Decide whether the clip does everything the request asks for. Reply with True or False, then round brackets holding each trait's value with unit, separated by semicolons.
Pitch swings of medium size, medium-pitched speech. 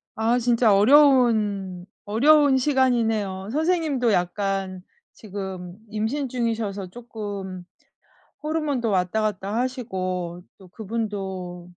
False (4.5 semitones; 215 Hz)